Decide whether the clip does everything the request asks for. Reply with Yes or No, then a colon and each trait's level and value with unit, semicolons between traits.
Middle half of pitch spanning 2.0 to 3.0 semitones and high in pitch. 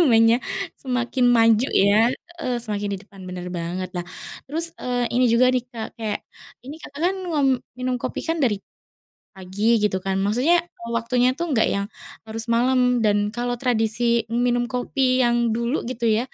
Yes: narrow, 2.5 semitones; high, 240 Hz